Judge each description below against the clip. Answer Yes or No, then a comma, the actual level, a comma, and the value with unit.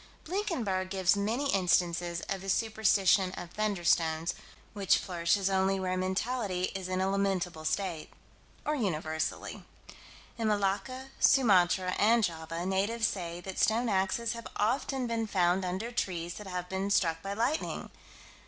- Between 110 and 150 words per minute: Yes, average, 140 wpm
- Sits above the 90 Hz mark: Yes, high, 190 Hz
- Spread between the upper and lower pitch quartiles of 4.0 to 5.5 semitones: No, average, 3.4 semitones